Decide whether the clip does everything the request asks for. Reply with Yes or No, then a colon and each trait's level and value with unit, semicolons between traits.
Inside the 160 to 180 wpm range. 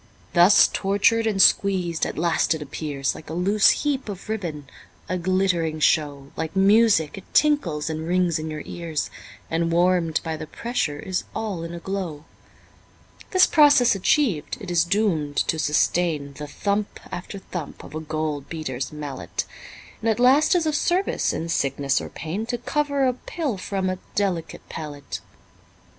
Yes: average, 165 wpm